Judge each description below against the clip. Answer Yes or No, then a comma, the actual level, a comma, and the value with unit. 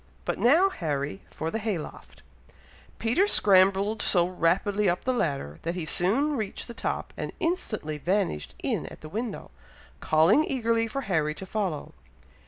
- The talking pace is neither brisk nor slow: Yes, average, 160 wpm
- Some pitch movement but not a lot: No, wide, 6.0 semitones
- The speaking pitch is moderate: No, high, 195 Hz